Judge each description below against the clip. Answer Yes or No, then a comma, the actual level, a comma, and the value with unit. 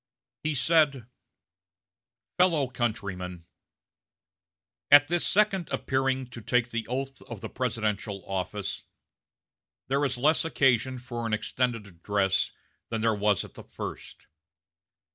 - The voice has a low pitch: Yes, low, 120 Hz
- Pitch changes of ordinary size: Yes, average, 4.5 semitones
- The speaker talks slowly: Yes, slow, 120 wpm